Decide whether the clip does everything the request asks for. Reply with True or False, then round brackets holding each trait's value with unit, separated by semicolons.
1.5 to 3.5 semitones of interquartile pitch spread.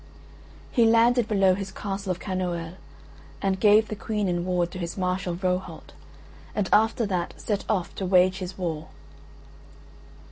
True (2.4 semitones)